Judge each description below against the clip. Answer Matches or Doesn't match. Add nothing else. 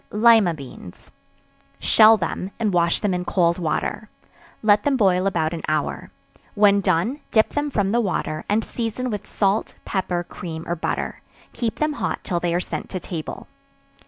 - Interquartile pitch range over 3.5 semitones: Matches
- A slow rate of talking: Doesn't match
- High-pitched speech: Matches